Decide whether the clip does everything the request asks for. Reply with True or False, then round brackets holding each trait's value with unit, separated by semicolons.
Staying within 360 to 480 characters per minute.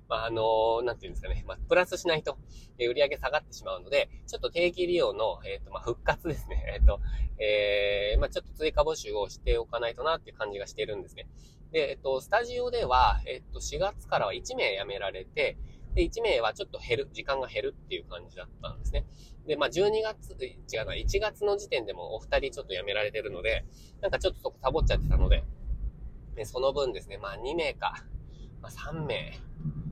True (415 characters per minute)